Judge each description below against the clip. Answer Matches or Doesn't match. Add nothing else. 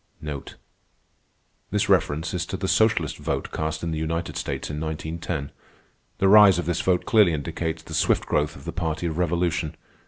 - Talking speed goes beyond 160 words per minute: Matches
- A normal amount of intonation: Doesn't match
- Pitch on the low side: Matches